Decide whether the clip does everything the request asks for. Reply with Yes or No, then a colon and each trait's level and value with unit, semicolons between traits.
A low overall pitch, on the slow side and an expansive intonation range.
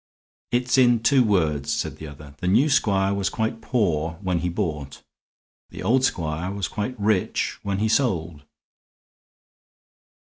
No: very low, 95 Hz; average, 145 wpm; wide, 5.9 semitones